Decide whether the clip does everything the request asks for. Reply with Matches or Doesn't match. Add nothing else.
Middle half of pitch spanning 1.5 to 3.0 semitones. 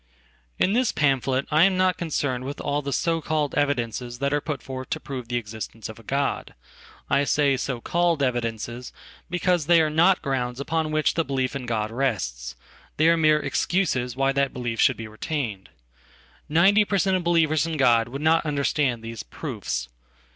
Doesn't match